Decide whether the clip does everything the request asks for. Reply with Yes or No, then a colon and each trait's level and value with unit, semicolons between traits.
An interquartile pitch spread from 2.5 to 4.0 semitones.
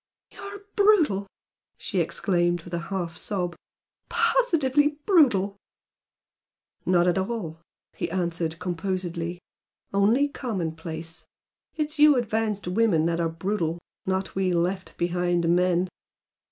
No: average, 5.2 semitones